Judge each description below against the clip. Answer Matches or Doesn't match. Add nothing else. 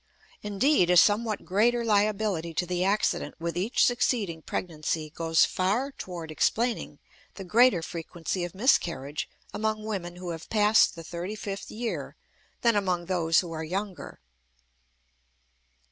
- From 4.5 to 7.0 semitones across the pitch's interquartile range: Doesn't match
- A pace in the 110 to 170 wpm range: Matches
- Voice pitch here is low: Doesn't match